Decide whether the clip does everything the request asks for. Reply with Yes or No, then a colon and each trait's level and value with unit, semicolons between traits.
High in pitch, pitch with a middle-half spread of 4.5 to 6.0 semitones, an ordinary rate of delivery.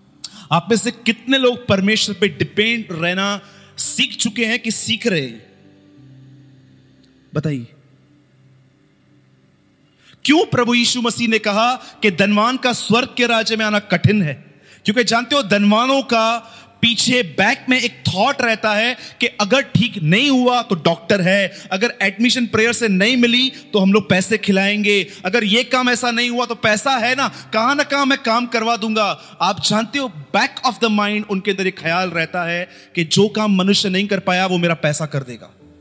Yes: high, 210 Hz; average, 5.1 semitones; average, 180 wpm